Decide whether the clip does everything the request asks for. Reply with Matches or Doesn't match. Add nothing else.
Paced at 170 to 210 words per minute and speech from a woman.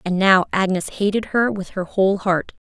Matches